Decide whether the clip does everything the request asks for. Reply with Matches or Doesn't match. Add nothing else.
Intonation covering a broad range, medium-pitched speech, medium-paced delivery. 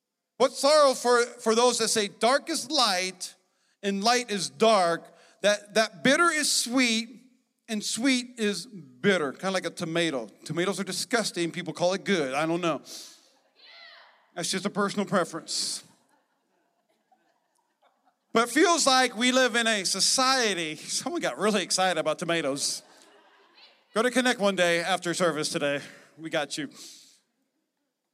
Doesn't match